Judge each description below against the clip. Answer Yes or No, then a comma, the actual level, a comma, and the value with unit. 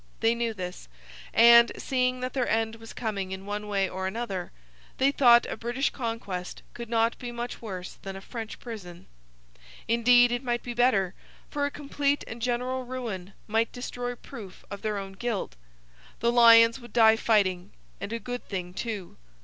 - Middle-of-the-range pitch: No, high, 230 Hz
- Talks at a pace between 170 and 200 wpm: Yes, average, 175 wpm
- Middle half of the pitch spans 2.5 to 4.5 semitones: Yes, average, 3.4 semitones